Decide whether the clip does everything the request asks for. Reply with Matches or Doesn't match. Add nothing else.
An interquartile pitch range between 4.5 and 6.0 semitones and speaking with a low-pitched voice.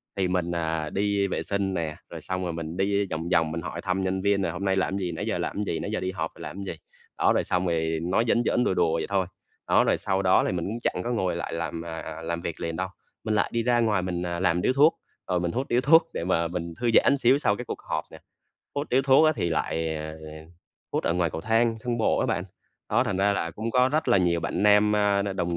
Doesn't match